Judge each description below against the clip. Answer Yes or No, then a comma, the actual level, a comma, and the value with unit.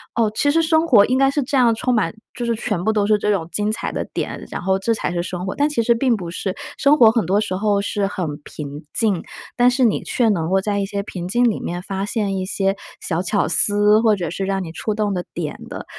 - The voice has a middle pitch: No, high, 205 Hz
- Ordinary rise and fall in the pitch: Yes, average, 3.7 semitones